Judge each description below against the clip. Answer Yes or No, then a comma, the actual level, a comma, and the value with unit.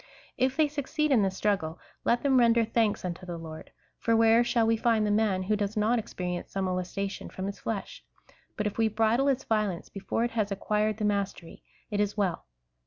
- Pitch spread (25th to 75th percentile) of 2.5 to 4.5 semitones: Yes, average, 2.8 semitones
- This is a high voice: Yes, high, 210 Hz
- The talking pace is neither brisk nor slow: No, fast, 210 wpm